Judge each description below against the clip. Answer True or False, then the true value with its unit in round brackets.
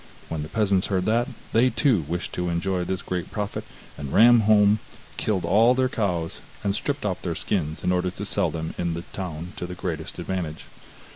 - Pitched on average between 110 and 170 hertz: False (90 Hz)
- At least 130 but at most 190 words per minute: False (200 wpm)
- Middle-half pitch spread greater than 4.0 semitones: False (3.7 semitones)